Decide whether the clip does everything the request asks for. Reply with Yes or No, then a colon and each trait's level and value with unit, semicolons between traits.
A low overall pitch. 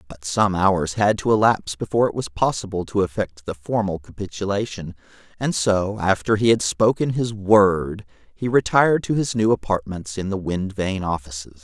Yes: low, 100 Hz